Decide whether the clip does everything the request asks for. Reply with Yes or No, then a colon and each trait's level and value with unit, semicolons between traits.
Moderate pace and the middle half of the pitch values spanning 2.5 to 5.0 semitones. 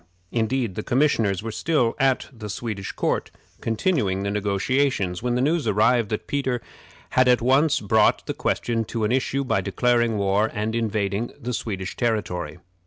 Yes: average, 165 wpm; average, 3.6 semitones